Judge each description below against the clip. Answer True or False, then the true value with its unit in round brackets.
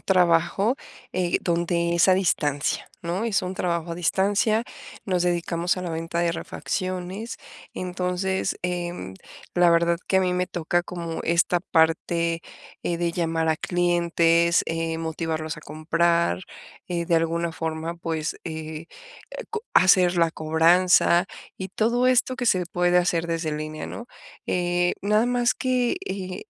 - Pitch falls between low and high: True (175 Hz)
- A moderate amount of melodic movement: False (1.7 semitones)